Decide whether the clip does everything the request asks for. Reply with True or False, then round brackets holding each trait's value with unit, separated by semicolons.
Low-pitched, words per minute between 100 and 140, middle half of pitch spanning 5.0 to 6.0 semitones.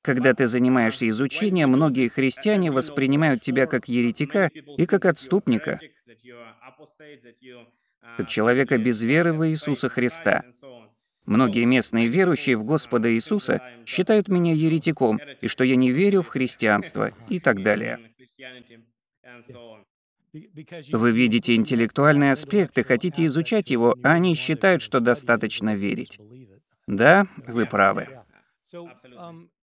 True (130 Hz; 115 wpm; 5.4 semitones)